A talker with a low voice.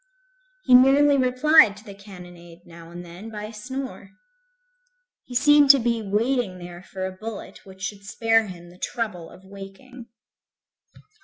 No: high, 210 Hz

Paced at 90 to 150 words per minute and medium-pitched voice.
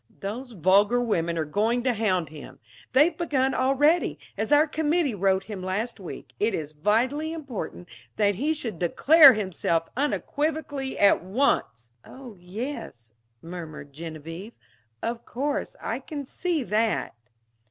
No: slow, 135 wpm; high, 225 Hz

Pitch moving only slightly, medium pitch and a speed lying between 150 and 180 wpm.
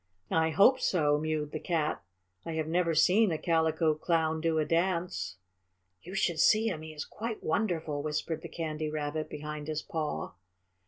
Yes: narrow, 1.9 semitones; medium, 160 Hz; average, 170 wpm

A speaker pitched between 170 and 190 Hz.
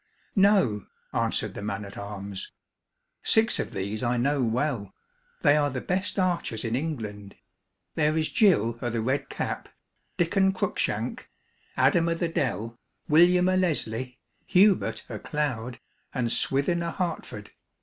No: medium, 140 Hz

